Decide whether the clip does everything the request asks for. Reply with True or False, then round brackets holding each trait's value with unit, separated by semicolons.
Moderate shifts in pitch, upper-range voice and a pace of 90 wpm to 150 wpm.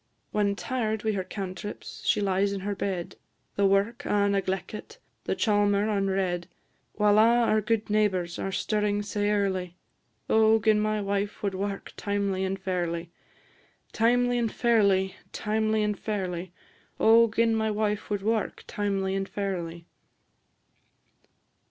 False (1.9 semitones; 205 Hz; 140 wpm)